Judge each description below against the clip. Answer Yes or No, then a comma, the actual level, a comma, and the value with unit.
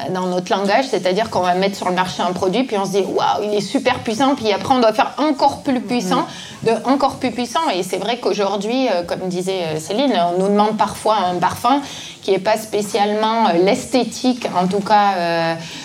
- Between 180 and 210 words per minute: Yes, average, 205 wpm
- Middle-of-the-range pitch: No, high, 205 Hz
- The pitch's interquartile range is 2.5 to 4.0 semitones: No, average, 4.5 semitones